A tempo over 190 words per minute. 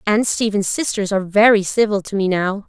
Yes: average, 200 wpm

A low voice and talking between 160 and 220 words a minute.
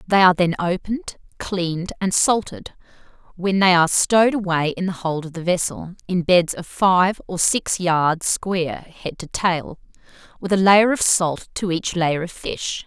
No: medium, 180 Hz; average, 180 wpm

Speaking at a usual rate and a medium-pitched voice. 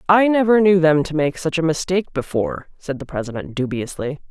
Yes: average, 195 wpm; medium, 160 Hz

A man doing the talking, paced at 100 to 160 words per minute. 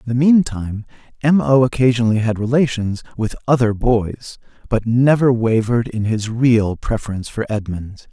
Yes: male; average, 150 wpm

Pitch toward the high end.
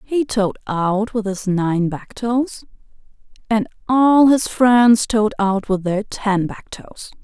Yes: high, 215 Hz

